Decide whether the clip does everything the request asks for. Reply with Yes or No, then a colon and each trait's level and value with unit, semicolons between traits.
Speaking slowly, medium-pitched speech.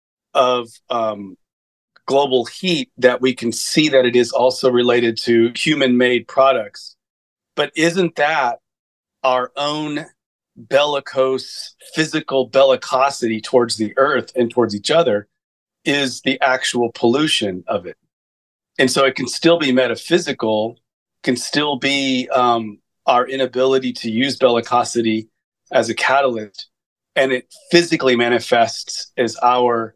No: slow, 125 wpm; low, 130 Hz